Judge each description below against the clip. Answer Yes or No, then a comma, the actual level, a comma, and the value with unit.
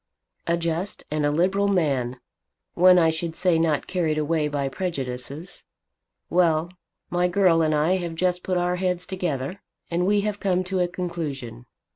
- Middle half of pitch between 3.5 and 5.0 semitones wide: No, average, 3.0 semitones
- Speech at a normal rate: Yes, average, 165 wpm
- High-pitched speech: No, medium, 170 Hz